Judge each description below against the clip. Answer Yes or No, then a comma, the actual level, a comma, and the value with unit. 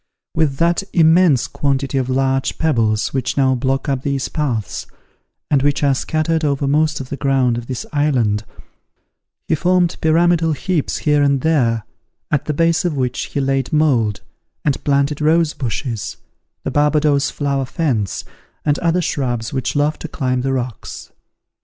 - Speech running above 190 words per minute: No, average, 160 wpm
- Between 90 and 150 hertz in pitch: Yes, medium, 140 Hz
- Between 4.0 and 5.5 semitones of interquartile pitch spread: No, average, 3.1 semitones